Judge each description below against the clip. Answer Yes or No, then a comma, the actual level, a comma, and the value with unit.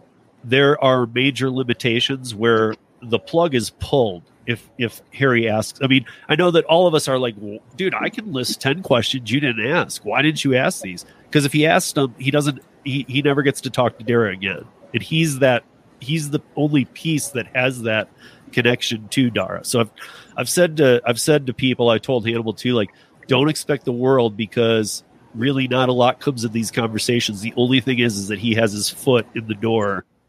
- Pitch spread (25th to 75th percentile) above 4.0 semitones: No, average, 3.2 semitones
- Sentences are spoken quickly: Yes, fast, 210 wpm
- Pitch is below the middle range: Yes, low, 125 Hz